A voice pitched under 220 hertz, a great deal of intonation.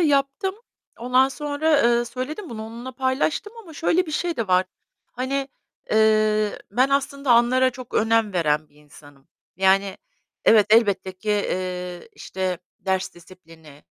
No: high, 225 Hz; wide, 6.5 semitones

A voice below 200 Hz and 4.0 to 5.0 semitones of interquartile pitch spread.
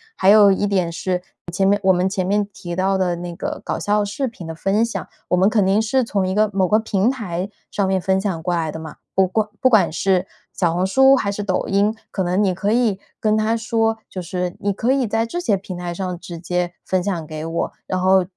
No: high, 190 Hz; average, 3.0 semitones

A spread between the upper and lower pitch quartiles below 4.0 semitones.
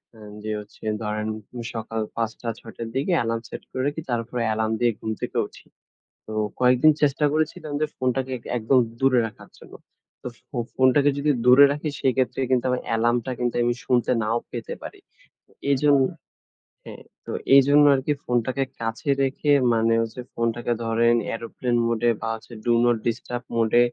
Yes: average, 2.9 semitones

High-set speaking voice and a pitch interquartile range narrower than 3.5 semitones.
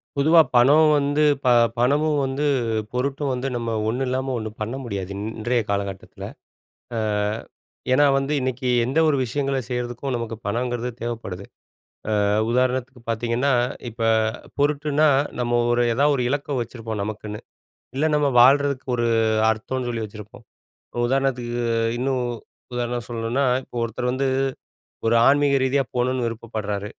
No: low, 125 Hz; average, 2.9 semitones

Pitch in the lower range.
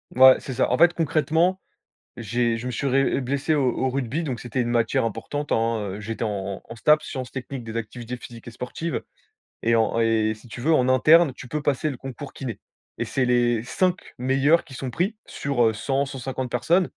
Yes: low, 125 Hz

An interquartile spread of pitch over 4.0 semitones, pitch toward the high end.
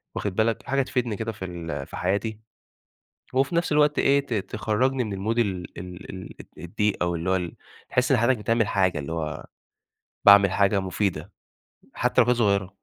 No: average, 4.5 semitones; low, 105 Hz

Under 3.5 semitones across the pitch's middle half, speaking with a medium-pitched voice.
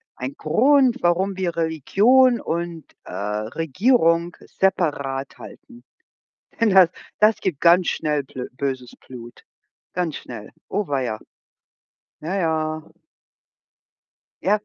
No: wide, 5.8 semitones; medium, 165 Hz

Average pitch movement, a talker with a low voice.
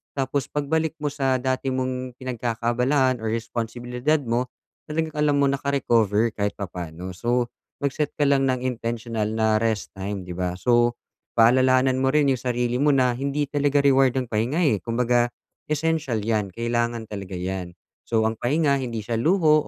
Yes: average, 3.5 semitones; low, 125 Hz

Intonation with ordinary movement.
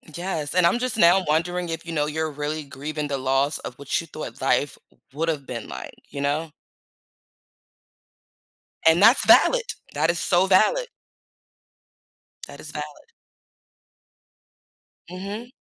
Yes: average, 3.8 semitones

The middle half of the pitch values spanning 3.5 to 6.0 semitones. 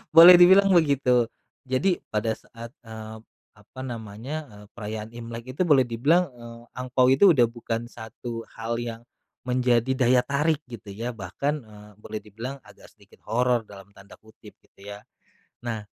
No: average, 2.8 semitones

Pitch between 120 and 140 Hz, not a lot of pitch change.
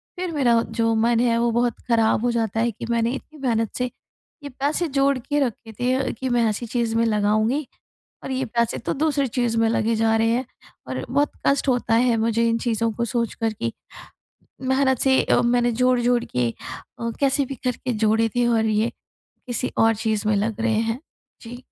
No: high, 235 Hz; narrow, 2.1 semitones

